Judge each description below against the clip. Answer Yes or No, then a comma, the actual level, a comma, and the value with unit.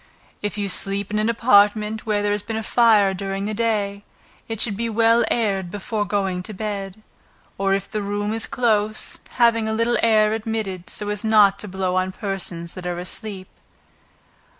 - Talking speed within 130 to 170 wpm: No, average, 180 wpm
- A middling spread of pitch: No, narrow, 2.1 semitones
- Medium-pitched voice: No, high, 205 Hz